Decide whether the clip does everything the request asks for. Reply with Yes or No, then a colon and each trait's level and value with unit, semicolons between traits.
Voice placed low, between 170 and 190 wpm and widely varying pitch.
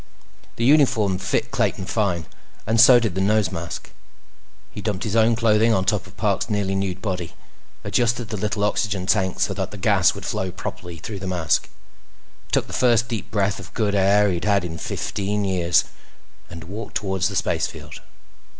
No: low, 100 Hz; average, 180 wpm; average, 2.7 semitones